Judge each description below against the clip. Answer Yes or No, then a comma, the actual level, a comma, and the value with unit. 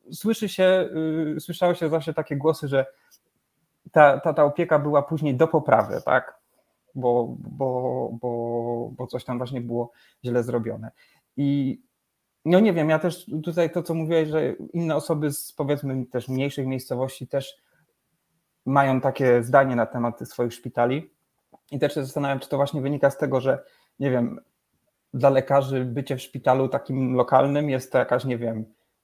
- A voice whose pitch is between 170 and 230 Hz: No, medium, 140 Hz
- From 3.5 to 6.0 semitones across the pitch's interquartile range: Yes, average, 3.8 semitones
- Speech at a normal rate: No, fast, 165 wpm